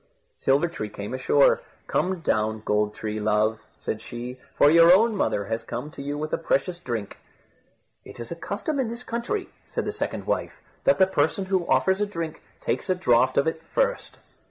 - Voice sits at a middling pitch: Yes, medium, 155 Hz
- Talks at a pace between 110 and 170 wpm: No, average, 200 wpm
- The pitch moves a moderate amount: No, wide, 8.5 semitones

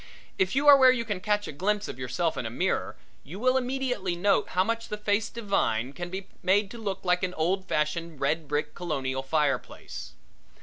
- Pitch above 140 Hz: Yes, medium, 185 Hz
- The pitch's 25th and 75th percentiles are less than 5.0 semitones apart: No, wide, 5.5 semitones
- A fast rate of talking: Yes, fast, 215 wpm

